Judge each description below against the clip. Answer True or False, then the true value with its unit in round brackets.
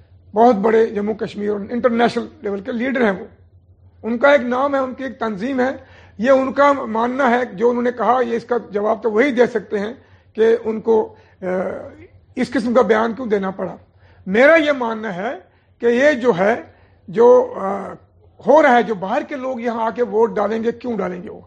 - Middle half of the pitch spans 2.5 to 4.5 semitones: True (3.0 semitones)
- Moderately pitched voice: False (230 Hz)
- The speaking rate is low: False (210 wpm)